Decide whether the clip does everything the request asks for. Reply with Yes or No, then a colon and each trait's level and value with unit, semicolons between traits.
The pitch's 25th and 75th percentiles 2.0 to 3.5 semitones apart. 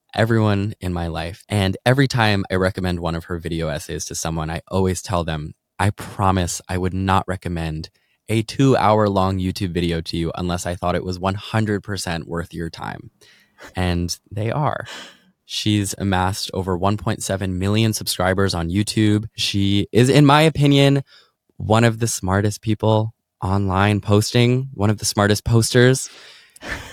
Yes: average, 3.2 semitones